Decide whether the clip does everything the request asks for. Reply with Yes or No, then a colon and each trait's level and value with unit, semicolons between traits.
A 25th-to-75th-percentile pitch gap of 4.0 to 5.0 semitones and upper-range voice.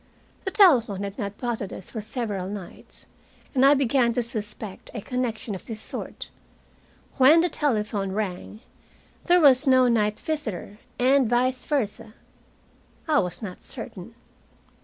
Yes: average, 4.3 semitones; high, 230 Hz